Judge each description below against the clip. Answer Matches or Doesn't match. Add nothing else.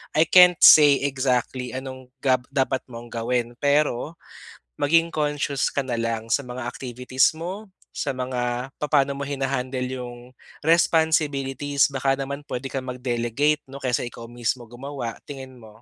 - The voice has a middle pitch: Doesn't match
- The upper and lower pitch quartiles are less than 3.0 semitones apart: Matches